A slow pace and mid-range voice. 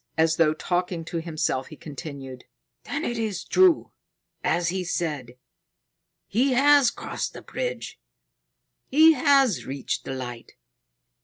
Yes: slow, 130 wpm; medium, 175 Hz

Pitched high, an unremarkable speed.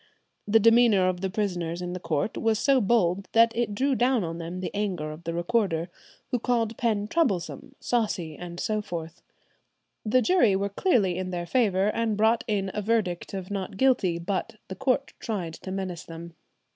Yes: high, 200 Hz; average, 185 wpm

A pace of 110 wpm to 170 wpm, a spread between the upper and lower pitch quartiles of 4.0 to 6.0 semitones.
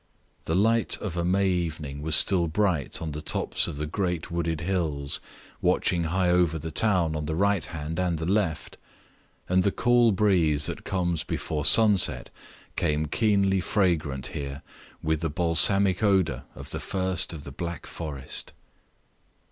No: average, 160 wpm; average, 3.6 semitones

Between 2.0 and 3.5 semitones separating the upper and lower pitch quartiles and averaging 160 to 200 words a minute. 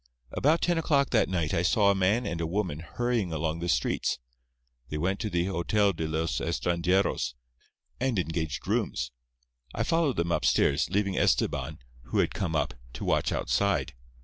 No: average, 4.5 semitones; average, 170 wpm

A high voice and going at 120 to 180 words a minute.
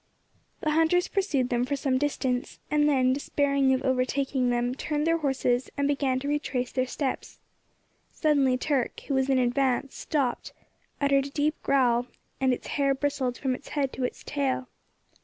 Yes: very high, 270 Hz; average, 170 wpm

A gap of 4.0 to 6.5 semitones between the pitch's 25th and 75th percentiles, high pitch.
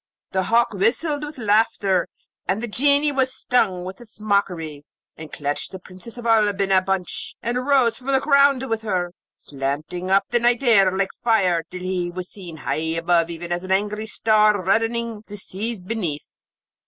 Yes: average, 4.5 semitones; high, 200 Hz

